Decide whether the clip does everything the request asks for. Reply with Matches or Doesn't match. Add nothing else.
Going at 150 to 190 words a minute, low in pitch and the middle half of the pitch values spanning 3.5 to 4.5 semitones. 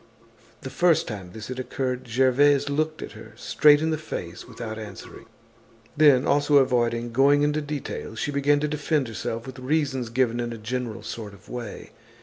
Matches